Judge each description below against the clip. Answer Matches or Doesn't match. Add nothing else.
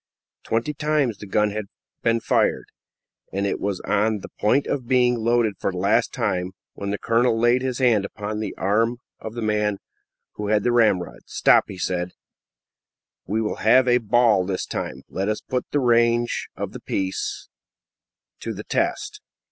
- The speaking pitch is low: Matches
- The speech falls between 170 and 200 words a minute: Matches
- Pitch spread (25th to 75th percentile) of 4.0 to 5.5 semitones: Doesn't match